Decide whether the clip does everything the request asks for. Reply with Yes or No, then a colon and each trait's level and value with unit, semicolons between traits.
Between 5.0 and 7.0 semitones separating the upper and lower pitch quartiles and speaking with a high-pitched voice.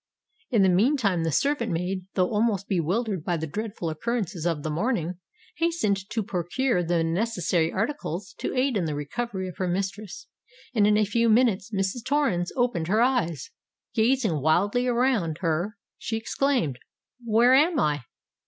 Yes: wide, 5.4 semitones; high, 200 Hz